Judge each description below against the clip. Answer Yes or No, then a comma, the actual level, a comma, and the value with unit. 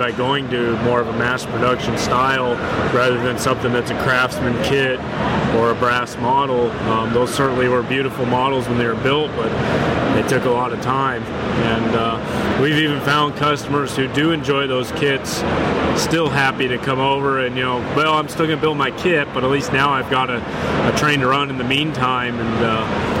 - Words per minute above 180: Yes, fast, 205 wpm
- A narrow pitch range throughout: Yes, narrow, 2.3 semitones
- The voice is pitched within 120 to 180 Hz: Yes, low, 130 Hz